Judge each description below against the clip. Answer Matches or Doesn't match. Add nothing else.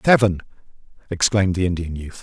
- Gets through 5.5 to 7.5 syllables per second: Matches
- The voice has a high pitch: Doesn't match